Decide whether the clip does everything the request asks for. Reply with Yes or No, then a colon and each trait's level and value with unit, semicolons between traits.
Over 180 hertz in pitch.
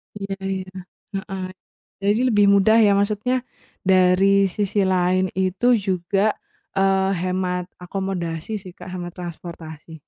Yes: high, 190 Hz